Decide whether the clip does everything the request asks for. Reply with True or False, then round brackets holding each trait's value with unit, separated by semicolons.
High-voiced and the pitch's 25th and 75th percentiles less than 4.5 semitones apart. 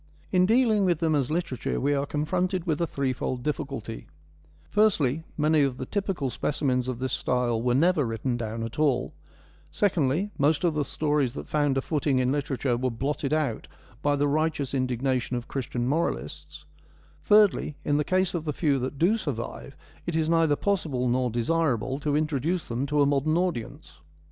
False (145 Hz; 4.0 semitones)